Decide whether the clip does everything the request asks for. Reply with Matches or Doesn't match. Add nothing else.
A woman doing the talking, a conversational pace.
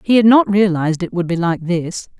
Doesn't match